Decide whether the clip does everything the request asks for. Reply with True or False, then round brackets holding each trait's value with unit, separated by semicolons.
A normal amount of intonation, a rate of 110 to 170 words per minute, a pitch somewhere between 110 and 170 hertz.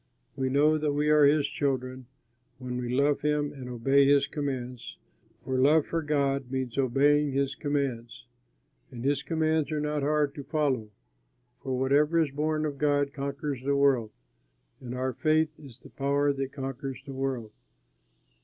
False (2.1 semitones; 165 wpm; 140 Hz)